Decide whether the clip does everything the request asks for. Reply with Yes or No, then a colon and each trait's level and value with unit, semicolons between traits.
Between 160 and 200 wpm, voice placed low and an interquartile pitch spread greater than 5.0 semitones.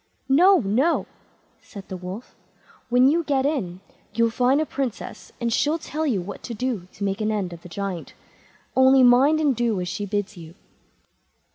No: average, 180 wpm; high, 230 Hz; wide, 5.6 semitones